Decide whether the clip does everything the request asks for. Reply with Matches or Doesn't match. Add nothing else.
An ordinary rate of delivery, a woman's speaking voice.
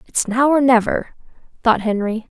Matches